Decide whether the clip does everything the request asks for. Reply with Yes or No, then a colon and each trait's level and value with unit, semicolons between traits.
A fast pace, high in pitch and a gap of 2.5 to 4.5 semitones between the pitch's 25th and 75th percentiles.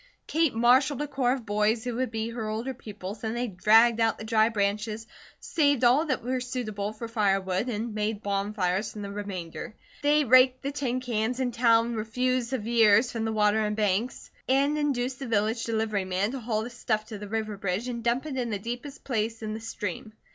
Yes: fast, 210 wpm; high, 225 Hz; average, 2.9 semitones